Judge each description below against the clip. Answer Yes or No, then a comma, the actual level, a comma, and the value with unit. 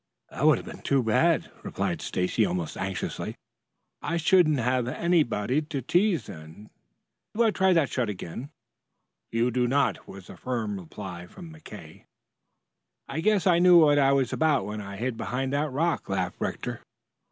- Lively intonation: Yes, wide, 7.4 semitones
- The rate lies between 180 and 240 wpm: No, average, 170 wpm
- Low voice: Yes, low, 130 Hz